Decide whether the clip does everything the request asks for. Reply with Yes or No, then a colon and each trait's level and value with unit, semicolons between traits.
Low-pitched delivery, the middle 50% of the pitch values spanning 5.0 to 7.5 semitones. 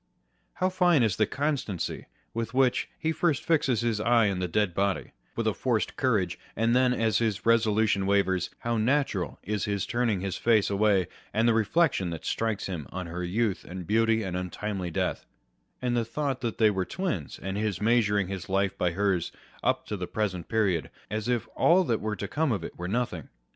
No: low, 105 Hz; average, 3.7 semitones